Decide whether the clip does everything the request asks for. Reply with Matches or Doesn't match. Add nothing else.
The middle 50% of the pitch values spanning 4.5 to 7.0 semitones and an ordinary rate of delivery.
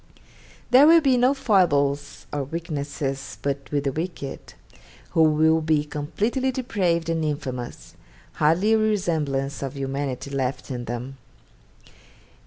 Doesn't match